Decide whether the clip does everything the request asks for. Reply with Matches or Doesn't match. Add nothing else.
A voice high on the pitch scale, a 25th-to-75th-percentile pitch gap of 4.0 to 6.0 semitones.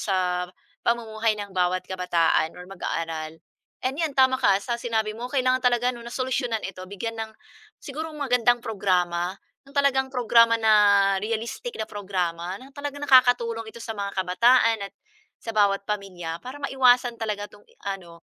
Matches